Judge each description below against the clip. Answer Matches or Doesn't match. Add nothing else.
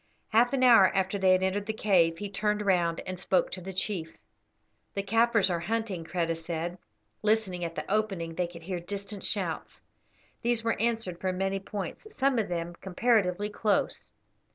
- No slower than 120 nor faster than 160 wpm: Doesn't match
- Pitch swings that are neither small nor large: Matches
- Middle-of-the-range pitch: Doesn't match